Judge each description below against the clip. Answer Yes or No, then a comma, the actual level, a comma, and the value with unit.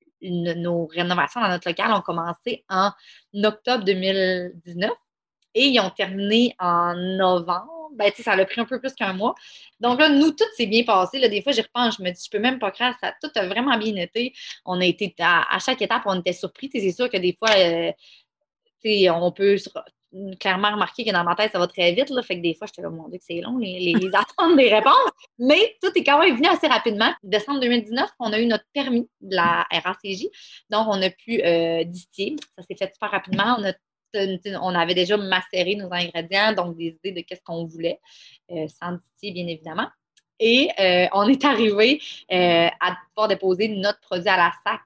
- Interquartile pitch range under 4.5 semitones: No, average, 4.9 semitones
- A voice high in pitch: Yes, high, 200 Hz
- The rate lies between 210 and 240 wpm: Yes, average, 215 wpm